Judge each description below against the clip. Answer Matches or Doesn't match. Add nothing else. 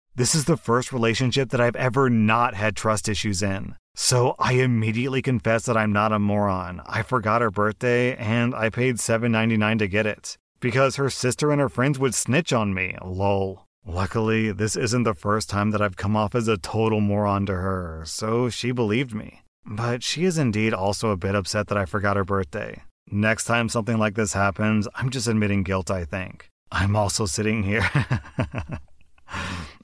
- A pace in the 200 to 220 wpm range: Doesn't match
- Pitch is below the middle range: Matches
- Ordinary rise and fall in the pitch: Matches